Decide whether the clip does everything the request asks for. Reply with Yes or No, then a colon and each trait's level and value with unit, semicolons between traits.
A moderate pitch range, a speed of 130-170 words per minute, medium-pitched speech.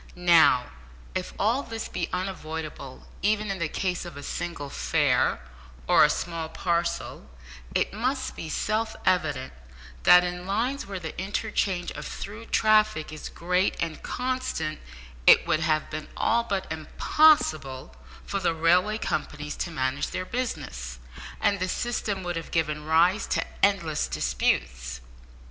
Yes: average, 4.7 semitones; average, 145 wpm; medium, 175 Hz